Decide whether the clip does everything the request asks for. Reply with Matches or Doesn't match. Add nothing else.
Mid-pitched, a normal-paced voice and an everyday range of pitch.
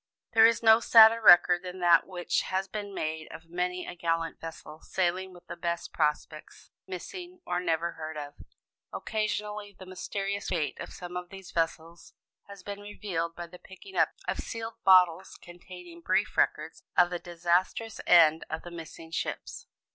Matches